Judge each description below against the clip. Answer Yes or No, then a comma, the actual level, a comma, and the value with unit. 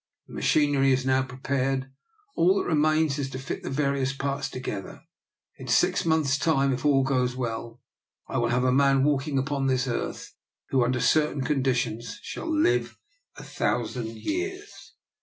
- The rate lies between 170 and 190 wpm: No, average, 160 wpm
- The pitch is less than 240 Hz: Yes, low, 135 Hz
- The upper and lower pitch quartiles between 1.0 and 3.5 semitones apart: Yes, narrow, 2.5 semitones